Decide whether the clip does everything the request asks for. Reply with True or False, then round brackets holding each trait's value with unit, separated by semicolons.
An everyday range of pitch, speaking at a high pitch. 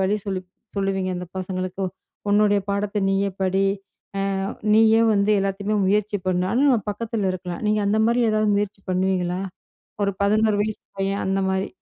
False (1.9 semitones; 200 Hz)